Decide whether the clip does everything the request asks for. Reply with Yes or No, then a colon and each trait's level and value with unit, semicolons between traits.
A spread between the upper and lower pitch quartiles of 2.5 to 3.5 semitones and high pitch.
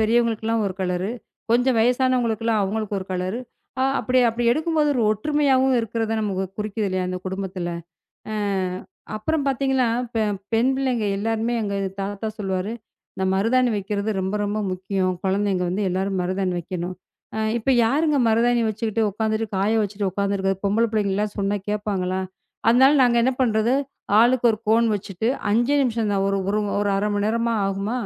Yes: average, 3.2 semitones; high, 215 Hz